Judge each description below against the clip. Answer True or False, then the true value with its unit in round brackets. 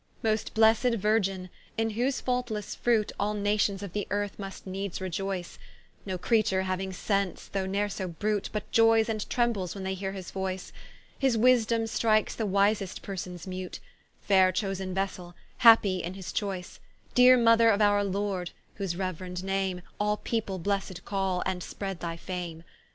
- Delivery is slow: False (160 wpm)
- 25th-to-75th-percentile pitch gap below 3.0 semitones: True (2.5 semitones)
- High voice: True (195 Hz)